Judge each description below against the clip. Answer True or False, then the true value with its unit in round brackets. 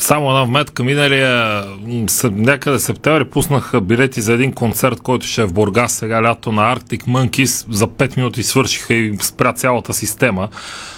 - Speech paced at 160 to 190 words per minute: True (165 wpm)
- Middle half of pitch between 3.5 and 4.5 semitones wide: False (2.6 semitones)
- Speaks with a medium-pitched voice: False (120 Hz)